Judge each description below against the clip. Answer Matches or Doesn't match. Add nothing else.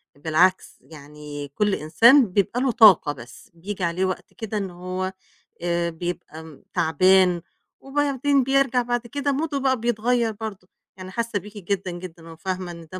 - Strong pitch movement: Matches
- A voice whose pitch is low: Doesn't match